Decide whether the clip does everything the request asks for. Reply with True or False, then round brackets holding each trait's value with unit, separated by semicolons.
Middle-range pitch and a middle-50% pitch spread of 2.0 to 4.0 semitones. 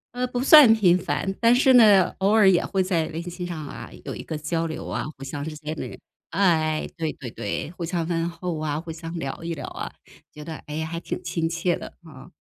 True (165 Hz; 2.9 semitones)